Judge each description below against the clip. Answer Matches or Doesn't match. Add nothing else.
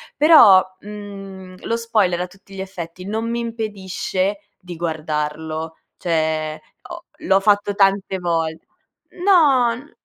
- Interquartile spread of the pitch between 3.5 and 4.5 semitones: Matches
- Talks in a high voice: Matches